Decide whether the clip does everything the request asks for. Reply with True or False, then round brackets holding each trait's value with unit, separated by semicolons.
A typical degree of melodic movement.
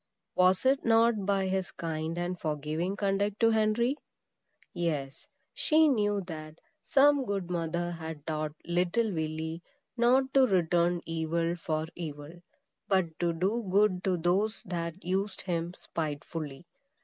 True (4.0 semitones)